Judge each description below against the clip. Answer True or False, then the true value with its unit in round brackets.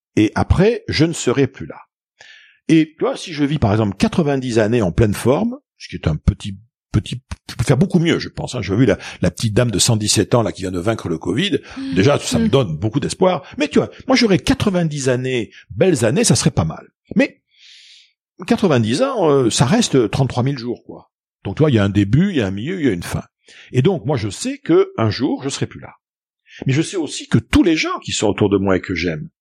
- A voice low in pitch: True (130 Hz)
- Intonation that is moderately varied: False (7.5 semitones)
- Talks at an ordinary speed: False (250 wpm)